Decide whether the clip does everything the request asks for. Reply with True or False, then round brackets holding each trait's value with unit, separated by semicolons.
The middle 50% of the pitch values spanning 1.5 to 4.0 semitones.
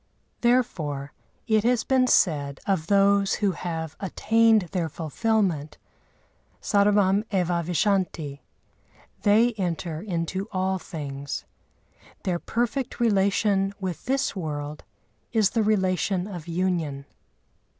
False (4.5 semitones)